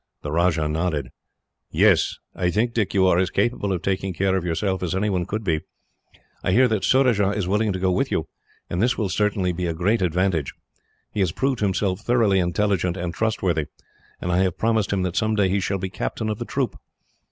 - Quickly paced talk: Yes, fast, 210 wpm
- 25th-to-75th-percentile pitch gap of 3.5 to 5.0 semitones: No, average, 2.9 semitones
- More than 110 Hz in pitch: No, very low, 95 Hz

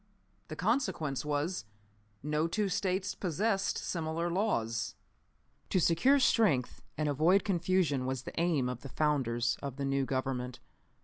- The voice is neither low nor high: Yes, medium, 155 Hz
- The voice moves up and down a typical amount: No, wide, 5.7 semitones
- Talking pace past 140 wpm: No, slow, 135 wpm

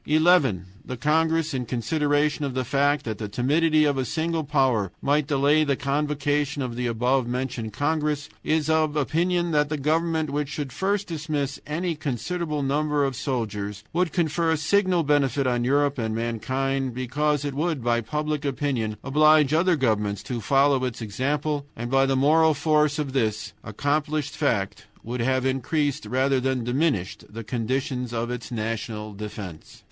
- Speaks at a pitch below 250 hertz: Yes, medium, 140 Hz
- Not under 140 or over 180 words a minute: Yes, average, 165 wpm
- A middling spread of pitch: Yes, average, 3.7 semitones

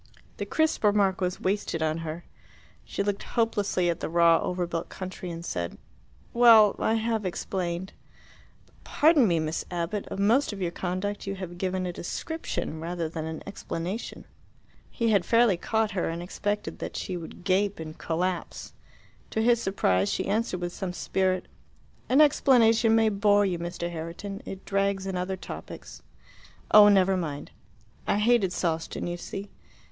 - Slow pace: No, average, 165 wpm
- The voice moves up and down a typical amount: Yes, average, 3.3 semitones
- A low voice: No, high, 190 Hz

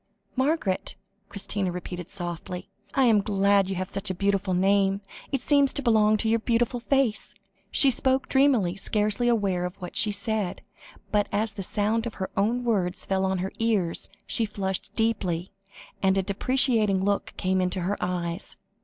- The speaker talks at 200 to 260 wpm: No, average, 170 wpm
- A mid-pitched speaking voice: No, high, 200 Hz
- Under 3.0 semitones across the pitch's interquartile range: No, average, 3.3 semitones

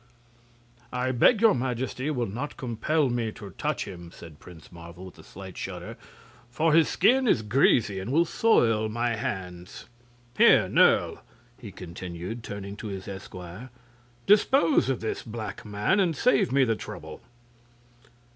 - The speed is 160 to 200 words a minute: No, average, 150 wpm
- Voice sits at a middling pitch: No, low, 115 Hz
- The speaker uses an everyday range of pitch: No, wide, 5.7 semitones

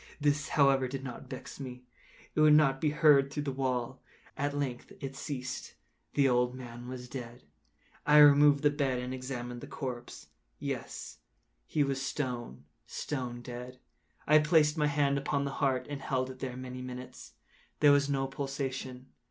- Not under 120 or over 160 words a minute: No, average, 170 wpm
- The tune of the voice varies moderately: No, narrow, 2.2 semitones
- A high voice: No, low, 135 Hz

